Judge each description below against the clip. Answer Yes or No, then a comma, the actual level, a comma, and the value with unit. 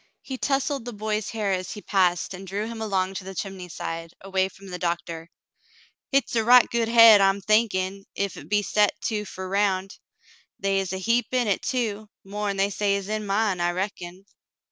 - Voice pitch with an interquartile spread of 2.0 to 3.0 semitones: Yes, narrow, 2.4 semitones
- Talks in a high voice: Yes, high, 200 Hz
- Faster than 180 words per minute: Yes, average, 195 wpm